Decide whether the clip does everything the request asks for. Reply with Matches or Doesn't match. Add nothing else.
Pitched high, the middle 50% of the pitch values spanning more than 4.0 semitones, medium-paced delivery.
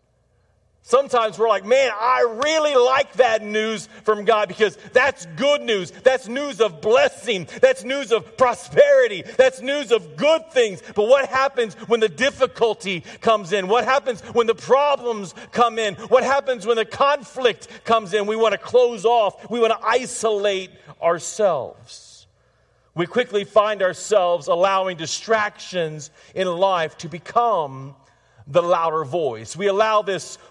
Matches